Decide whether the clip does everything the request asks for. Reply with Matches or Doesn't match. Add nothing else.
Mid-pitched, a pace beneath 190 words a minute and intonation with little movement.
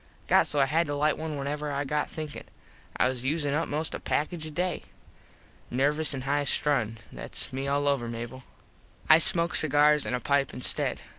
Doesn't match